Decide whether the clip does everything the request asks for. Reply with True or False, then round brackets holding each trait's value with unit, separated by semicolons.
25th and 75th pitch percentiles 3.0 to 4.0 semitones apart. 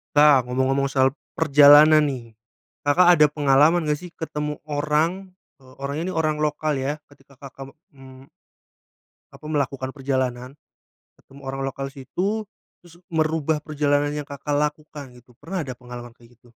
False (2.4 semitones)